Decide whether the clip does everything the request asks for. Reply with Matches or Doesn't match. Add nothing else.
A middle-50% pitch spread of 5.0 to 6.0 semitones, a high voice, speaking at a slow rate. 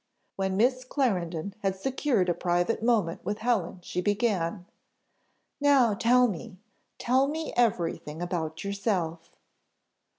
Matches